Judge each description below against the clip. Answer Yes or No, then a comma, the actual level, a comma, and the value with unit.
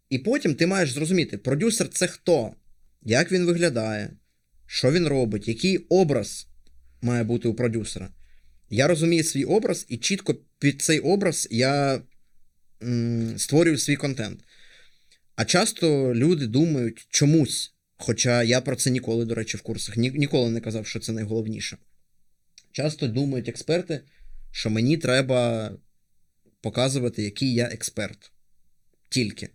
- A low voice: Yes, low, 120 Hz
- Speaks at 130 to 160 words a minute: Yes, average, 135 wpm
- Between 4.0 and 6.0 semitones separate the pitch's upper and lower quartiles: Yes, wide, 5.4 semitones